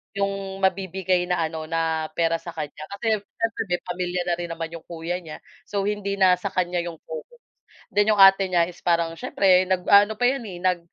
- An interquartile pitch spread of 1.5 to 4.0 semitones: Yes, average, 2.8 semitones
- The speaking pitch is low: No, medium, 180 Hz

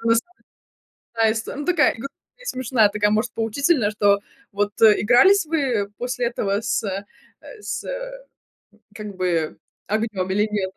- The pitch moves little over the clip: No, average, 3.4 semitones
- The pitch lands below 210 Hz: No, high, 220 Hz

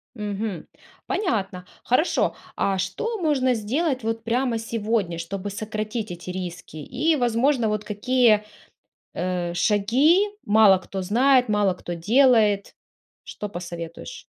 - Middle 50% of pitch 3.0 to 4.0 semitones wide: No, average, 4.7 semitones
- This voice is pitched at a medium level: No, high, 215 Hz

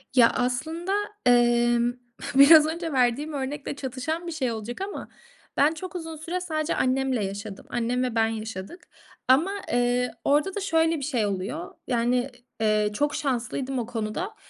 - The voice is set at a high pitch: Yes, very high, 260 Hz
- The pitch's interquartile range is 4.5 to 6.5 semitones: Yes, average, 4.9 semitones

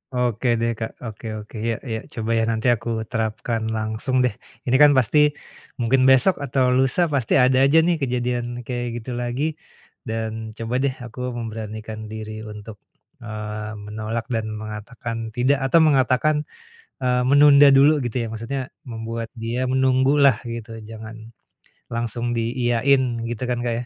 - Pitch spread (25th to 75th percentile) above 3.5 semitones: No, narrow, 2.6 semitones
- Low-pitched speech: Yes, low, 120 Hz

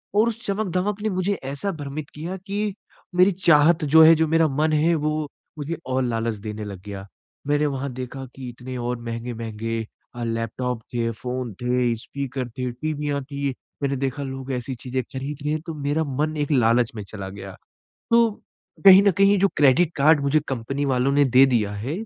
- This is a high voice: No, low, 135 Hz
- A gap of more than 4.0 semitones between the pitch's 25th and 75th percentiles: Yes, average, 4.4 semitones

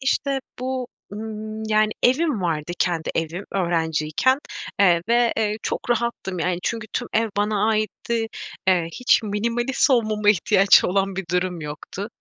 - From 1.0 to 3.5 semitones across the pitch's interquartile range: No, average, 4.5 semitones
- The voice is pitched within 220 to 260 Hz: No, high, 210 Hz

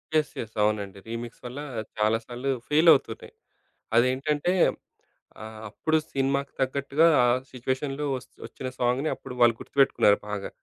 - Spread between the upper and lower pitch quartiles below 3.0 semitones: No, average, 3.3 semitones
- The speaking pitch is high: No, low, 130 Hz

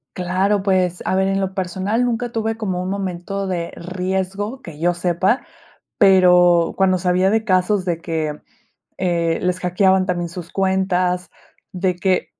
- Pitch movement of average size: No, narrow, 1.5 semitones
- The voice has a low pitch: No, medium, 185 Hz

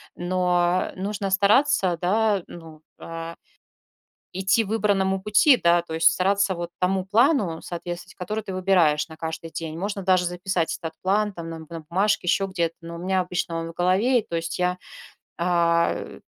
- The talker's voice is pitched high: No, medium, 180 Hz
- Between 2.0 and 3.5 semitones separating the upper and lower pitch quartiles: Yes, average, 2.7 semitones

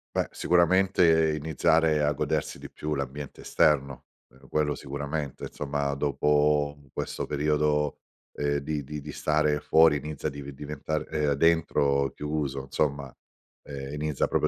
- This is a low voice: Yes, very low, 75 Hz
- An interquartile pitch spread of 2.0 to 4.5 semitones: No, narrow, 1.5 semitones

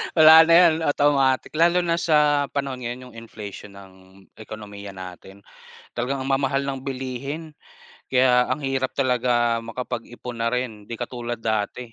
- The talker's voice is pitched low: Yes, low, 125 Hz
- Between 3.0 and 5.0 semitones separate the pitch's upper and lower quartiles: Yes, average, 3.4 semitones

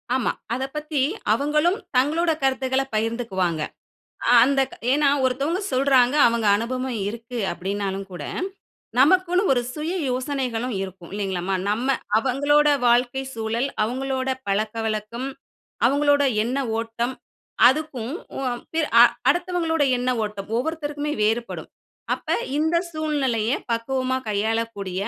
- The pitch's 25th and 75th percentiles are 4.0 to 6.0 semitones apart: Yes, average, 4.4 semitones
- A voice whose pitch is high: Yes, very high, 255 Hz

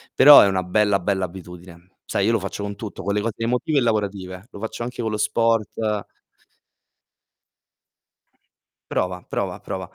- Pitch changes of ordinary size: Yes, average, 3.4 semitones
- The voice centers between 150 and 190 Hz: No, low, 100 Hz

